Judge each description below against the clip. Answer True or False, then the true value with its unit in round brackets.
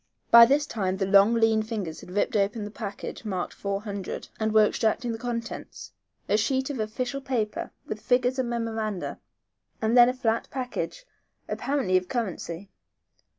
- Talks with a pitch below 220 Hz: False (225 Hz)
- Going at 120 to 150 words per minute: False (165 wpm)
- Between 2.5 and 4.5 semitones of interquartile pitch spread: True (3.2 semitones)